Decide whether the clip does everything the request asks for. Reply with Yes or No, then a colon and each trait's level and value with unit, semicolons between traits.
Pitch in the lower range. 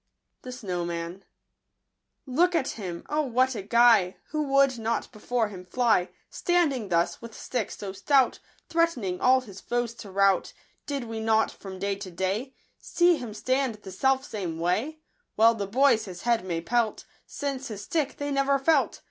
No: high, 230 Hz